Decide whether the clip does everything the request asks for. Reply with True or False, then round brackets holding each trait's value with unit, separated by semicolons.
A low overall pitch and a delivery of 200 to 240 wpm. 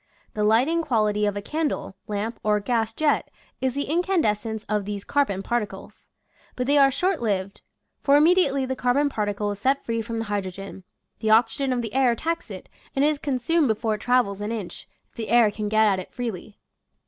False (230 Hz; 205 wpm)